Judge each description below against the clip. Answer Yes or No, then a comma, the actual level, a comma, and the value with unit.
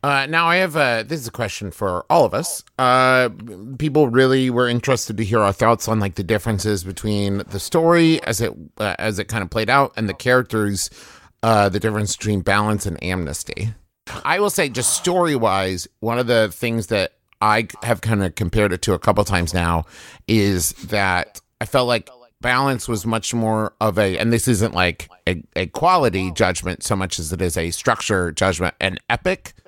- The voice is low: Yes, low, 110 Hz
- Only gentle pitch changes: No, average, 4.0 semitones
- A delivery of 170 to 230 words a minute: Yes, average, 200 wpm